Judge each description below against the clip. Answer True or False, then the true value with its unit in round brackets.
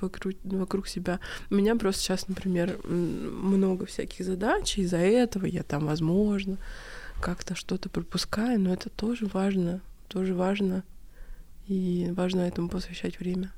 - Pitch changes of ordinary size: False (1.4 semitones)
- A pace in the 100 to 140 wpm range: True (135 wpm)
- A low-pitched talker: False (190 Hz)